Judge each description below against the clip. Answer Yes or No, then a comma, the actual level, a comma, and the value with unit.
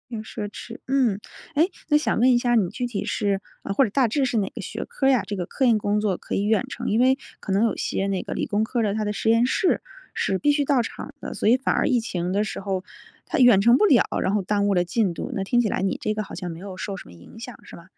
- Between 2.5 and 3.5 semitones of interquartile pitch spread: No, average, 3.9 semitones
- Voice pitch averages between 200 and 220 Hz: Yes, high, 215 Hz